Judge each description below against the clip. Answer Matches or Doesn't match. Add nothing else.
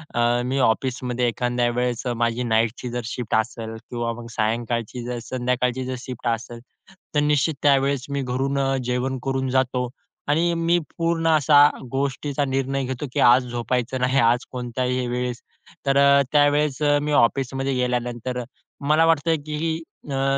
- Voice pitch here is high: Doesn't match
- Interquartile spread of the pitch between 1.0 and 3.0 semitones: Matches